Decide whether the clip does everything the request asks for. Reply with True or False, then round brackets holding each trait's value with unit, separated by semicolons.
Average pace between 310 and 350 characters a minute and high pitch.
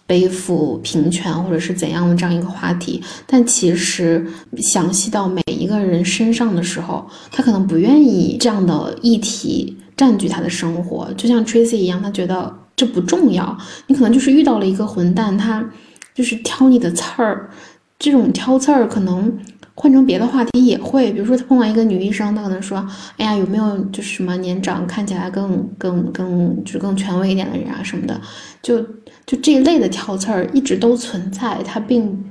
False (295 characters per minute; 200 Hz)